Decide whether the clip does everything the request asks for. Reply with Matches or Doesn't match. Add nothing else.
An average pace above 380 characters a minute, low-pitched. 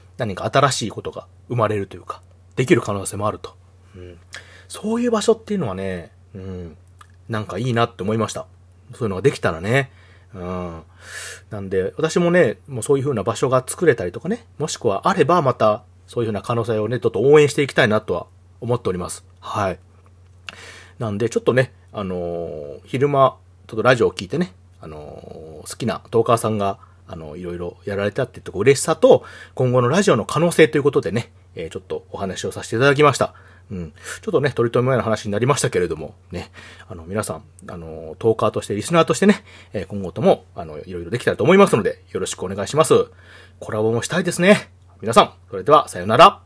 Matches